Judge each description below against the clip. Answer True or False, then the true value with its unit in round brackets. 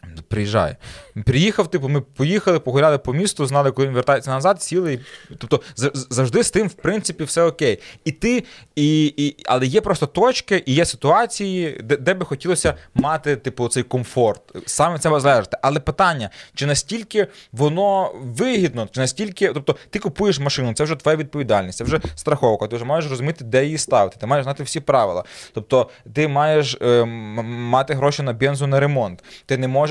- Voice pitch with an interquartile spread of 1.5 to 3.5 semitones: False (4.7 semitones)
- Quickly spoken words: True (175 wpm)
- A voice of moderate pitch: True (145 Hz)